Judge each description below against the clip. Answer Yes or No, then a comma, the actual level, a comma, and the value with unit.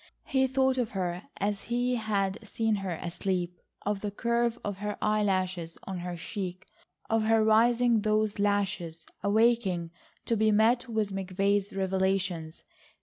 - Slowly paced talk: No, average, 145 wpm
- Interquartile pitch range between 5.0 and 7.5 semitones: No, average, 2.9 semitones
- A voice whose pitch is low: No, high, 205 Hz